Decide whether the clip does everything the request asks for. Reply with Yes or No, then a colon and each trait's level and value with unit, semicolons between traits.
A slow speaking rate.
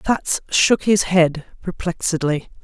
Yes: slow, 115 wpm